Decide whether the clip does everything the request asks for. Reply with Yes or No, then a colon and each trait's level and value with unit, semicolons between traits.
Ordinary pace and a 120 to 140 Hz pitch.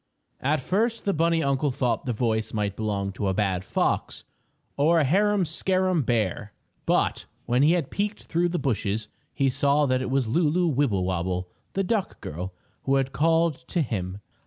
Yes: average, 175 wpm; low, 135 Hz